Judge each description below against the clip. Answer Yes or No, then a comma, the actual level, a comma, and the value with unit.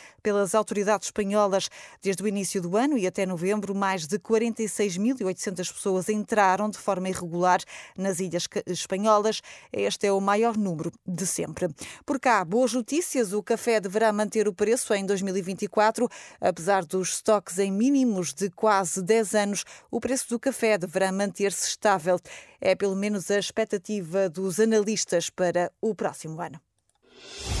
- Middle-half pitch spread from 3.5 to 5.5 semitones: No, narrow, 2.5 semitones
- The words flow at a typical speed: Yes, average, 150 wpm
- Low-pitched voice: No, high, 200 Hz